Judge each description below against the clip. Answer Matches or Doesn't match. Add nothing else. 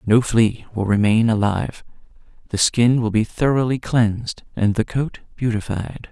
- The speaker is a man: Matches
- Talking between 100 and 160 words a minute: Matches